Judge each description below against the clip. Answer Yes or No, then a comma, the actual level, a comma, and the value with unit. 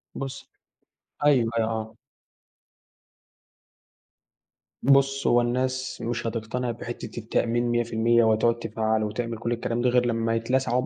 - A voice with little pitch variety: Yes, narrow, 1.6 semitones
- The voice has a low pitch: Yes, low, 120 Hz